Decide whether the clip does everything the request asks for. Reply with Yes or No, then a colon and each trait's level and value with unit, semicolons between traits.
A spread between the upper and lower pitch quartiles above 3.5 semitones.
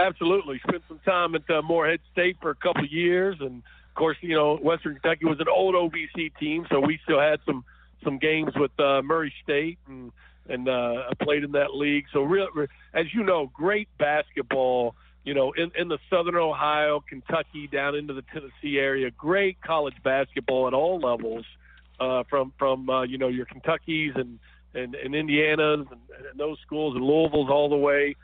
No: average, 3.2 semitones